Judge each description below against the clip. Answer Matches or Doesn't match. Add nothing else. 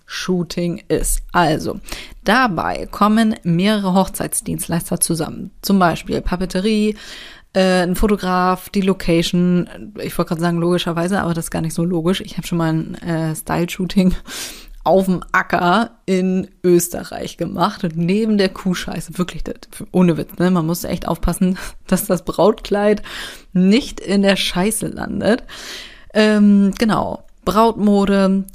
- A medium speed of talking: Matches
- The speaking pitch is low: Doesn't match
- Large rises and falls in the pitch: Doesn't match